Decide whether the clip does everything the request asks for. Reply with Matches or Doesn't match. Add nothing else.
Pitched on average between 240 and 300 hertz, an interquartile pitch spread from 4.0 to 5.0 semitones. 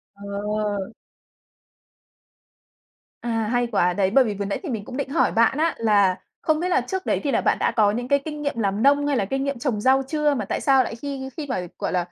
Doesn't match